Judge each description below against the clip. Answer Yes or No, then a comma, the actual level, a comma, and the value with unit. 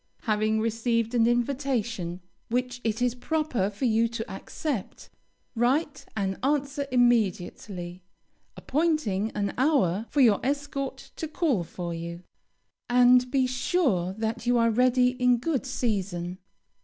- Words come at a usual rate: No, slow, 130 wpm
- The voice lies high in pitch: Yes, high, 240 Hz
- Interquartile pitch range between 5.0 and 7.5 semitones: No, average, 4.2 semitones